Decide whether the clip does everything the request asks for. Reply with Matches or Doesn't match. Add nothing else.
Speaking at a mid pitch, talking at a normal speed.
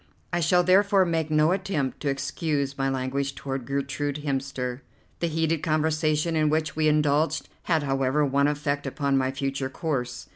Matches